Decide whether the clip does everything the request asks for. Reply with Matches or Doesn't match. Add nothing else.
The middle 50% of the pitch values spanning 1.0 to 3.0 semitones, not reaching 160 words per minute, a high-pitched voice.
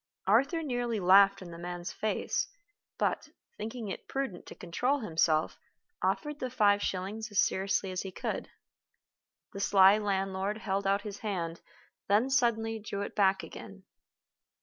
Matches